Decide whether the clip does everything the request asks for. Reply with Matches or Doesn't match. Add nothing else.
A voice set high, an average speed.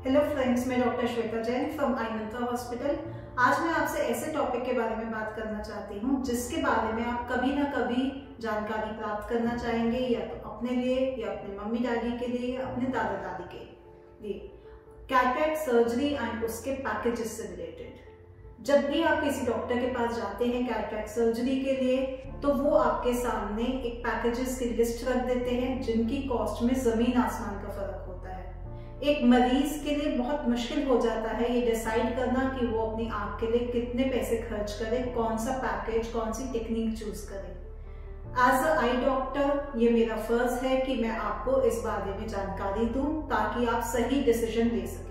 Matches